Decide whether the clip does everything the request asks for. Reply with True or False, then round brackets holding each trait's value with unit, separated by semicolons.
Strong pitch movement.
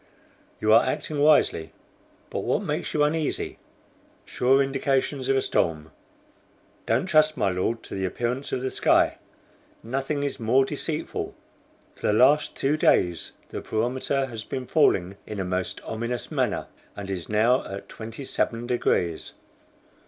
False (4.5 semitones)